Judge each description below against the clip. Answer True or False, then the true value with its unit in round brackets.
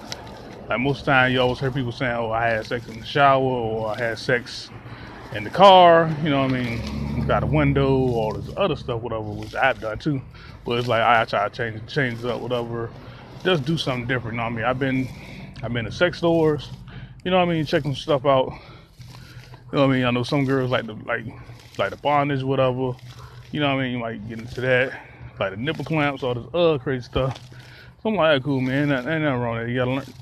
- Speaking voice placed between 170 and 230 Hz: False (130 Hz)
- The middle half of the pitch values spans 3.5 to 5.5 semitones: False (2.8 semitones)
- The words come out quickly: True (255 wpm)